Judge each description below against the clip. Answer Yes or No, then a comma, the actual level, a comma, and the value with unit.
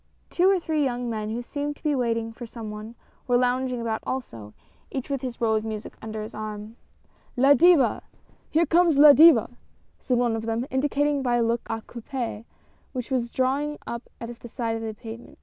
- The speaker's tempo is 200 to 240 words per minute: Yes, fast, 205 wpm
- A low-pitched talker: No, high, 240 Hz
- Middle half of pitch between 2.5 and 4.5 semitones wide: Yes, average, 3.6 semitones